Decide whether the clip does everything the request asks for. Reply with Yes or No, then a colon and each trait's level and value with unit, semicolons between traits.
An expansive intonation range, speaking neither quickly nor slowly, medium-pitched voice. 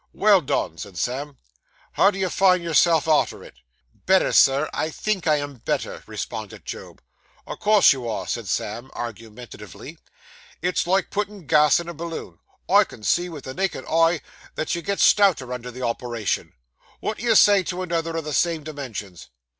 Yes: wide, 6.4 semitones; average, 180 wpm; medium, 155 Hz